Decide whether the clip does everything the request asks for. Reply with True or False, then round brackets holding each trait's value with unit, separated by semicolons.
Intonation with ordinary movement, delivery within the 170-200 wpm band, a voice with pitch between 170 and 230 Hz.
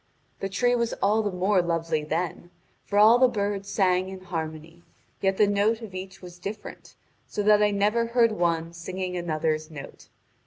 True (3.5 semitones; 180 wpm; 190 Hz)